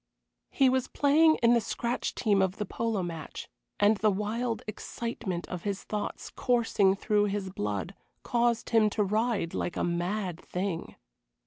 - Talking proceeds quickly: No, average, 155 wpm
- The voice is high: Yes, high, 210 Hz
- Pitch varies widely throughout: No, average, 3.7 semitones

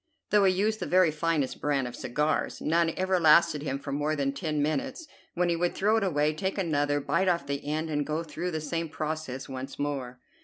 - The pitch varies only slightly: No, average, 3.3 semitones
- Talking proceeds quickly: Yes, fast, 220 wpm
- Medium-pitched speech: Yes, medium, 155 Hz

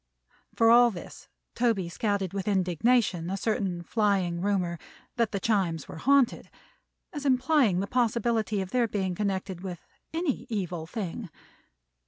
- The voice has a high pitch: Yes, high, 200 Hz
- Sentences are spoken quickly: No, average, 140 wpm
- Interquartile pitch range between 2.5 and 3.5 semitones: No, average, 4.4 semitones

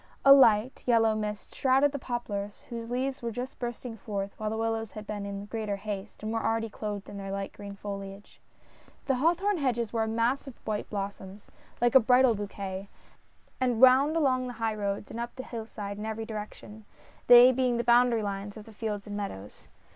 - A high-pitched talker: Yes, high, 225 Hz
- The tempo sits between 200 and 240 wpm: Yes, fast, 205 wpm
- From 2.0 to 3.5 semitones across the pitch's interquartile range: Yes, average, 3.2 semitones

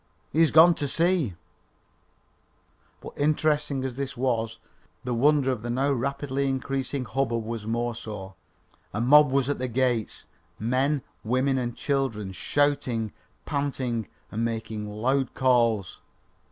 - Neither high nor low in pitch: No, low, 130 Hz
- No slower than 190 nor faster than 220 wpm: No, average, 140 wpm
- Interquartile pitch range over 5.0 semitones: No, average, 3.3 semitones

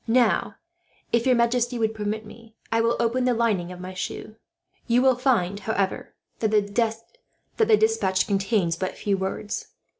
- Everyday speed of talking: Yes, average, 160 wpm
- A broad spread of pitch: No, average, 3.1 semitones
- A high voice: Yes, high, 225 Hz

